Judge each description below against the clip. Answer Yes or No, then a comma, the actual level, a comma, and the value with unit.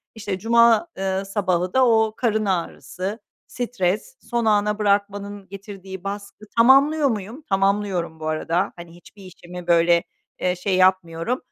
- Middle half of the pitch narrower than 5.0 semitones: Yes, average, 3.2 semitones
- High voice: Yes, high, 200 Hz